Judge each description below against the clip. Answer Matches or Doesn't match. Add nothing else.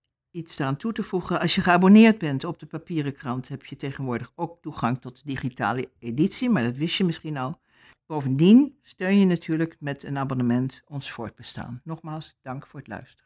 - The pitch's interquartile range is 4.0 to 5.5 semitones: Matches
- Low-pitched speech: Doesn't match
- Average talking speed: Matches